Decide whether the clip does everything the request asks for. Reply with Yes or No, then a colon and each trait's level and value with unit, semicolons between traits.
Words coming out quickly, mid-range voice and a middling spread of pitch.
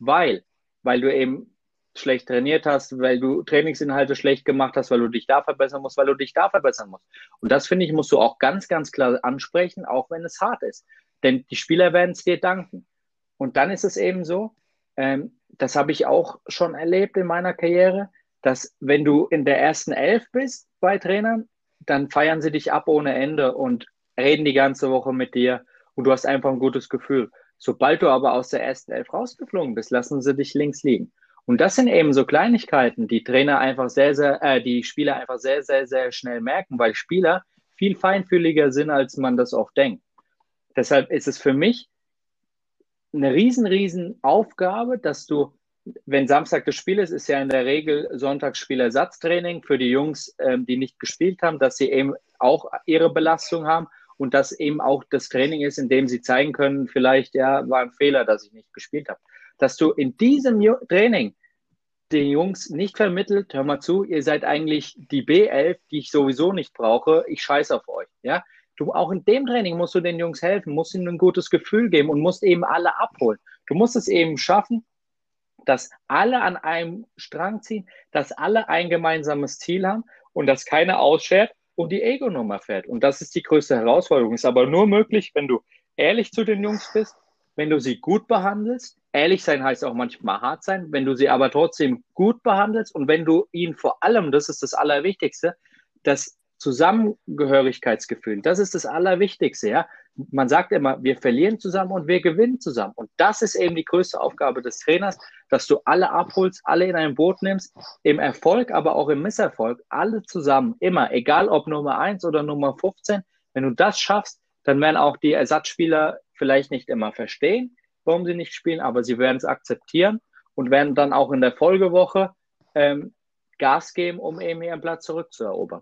No: fast, 195 wpm; medium, 160 Hz; wide, 6.1 semitones